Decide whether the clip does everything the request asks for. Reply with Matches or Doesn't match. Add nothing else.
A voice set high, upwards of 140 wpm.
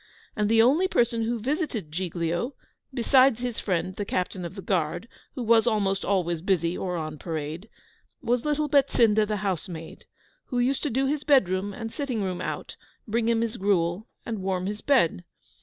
Matches